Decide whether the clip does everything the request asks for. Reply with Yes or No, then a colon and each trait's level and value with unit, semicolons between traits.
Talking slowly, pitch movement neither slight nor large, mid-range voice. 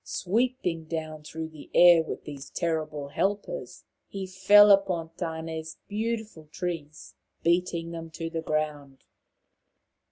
Yes: slow, 120 wpm; average, 3.3 semitones; medium, 165 Hz